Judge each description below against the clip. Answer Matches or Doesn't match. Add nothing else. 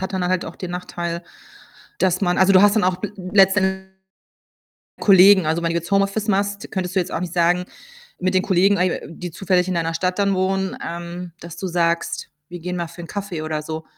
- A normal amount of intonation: Doesn't match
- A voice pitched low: Doesn't match